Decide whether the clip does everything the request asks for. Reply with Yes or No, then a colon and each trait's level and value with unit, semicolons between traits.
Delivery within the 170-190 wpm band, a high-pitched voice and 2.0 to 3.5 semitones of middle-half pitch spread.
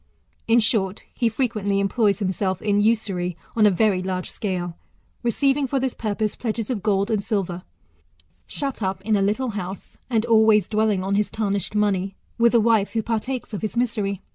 Yes: average, 180 wpm; high, 210 Hz; average, 2.7 semitones